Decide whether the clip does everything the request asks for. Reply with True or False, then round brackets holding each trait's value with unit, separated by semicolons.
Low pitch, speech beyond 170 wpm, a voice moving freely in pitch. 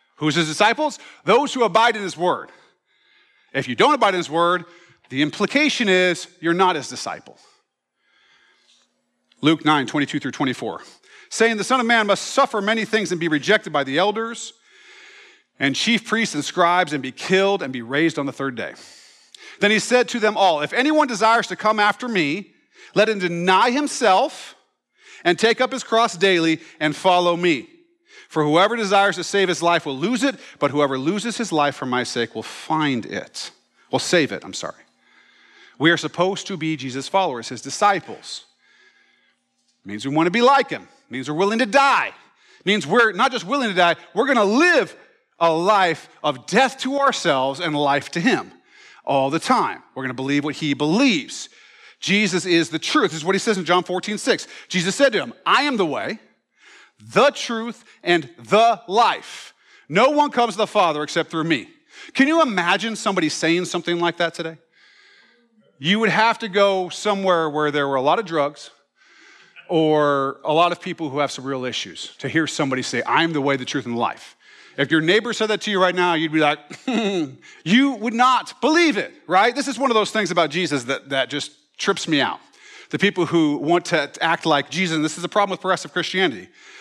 False (185 Hz; 200 wpm; 7.2 semitones)